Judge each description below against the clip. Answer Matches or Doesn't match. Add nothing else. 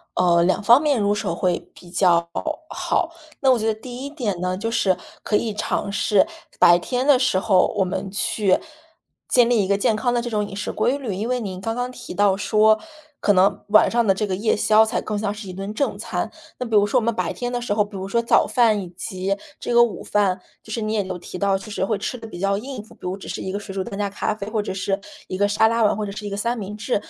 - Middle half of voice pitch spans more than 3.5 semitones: Doesn't match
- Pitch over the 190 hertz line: Matches